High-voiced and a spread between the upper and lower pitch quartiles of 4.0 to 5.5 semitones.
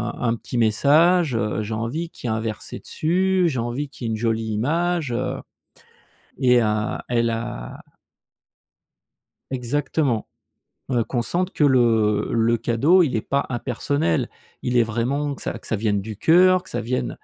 No: low, 120 Hz; average, 4.6 semitones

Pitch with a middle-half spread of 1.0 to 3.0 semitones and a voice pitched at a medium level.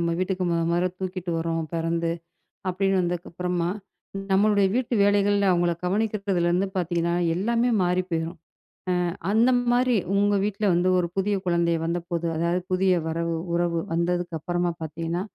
Yes: narrow, 2.4 semitones; medium, 180 Hz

